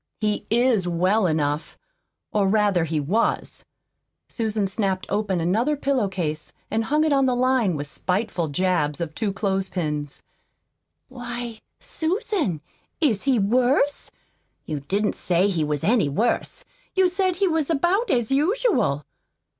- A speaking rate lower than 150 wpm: Yes, average, 140 wpm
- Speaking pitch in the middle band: No, high, 210 Hz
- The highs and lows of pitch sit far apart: Yes, wide, 6.9 semitones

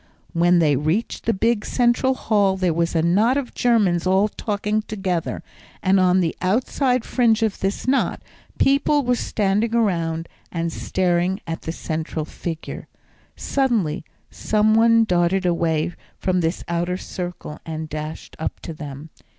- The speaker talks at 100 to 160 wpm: Yes, average, 150 wpm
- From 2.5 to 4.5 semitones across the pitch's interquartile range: No, average, 4.9 semitones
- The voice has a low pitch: No, medium, 185 Hz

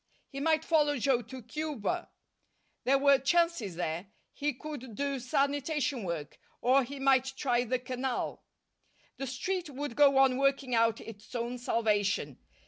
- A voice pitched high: Yes, very high, 265 Hz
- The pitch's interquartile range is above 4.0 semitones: No, average, 3.2 semitones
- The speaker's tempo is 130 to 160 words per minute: Yes, average, 145 wpm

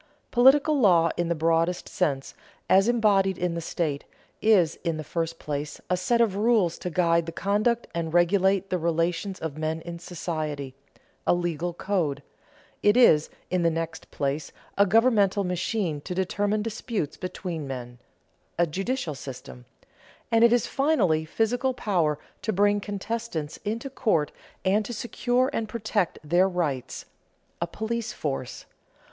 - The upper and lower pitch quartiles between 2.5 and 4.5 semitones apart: No, average, 4.9 semitones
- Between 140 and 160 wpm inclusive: Yes, average, 150 wpm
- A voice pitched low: No, medium, 180 Hz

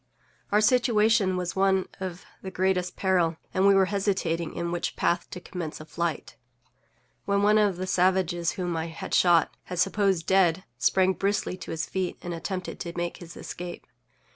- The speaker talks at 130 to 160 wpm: No, average, 170 wpm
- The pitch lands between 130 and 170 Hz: No, medium, 185 Hz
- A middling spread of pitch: No, narrow, 2.1 semitones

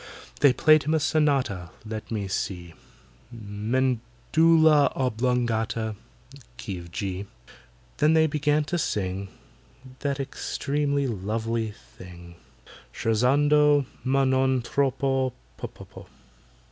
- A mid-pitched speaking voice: No, low, 125 Hz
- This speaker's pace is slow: Yes, slow, 90 wpm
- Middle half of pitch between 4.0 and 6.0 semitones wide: Yes, average, 5.1 semitones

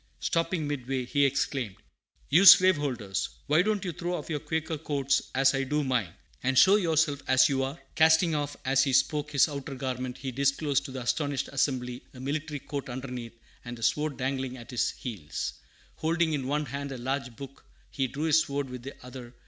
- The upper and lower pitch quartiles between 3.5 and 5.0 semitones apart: No, average, 2.7 semitones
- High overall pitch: No, medium, 140 Hz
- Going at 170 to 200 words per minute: Yes, average, 195 wpm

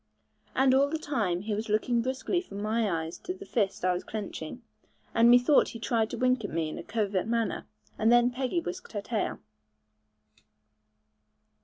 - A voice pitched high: Yes, high, 230 Hz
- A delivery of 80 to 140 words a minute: No, average, 180 wpm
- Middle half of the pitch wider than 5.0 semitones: No, average, 3.8 semitones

